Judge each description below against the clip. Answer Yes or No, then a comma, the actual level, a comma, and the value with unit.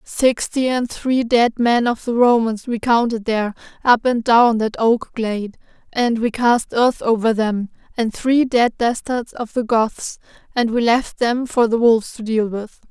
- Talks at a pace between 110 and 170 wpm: No, average, 185 wpm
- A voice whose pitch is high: Yes, high, 230 Hz